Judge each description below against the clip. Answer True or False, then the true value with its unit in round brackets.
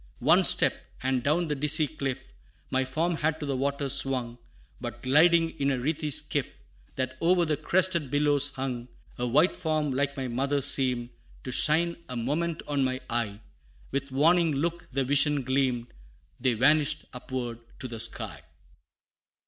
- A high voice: False (140 Hz)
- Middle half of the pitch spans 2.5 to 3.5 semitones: True (3.0 semitones)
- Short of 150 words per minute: False (160 wpm)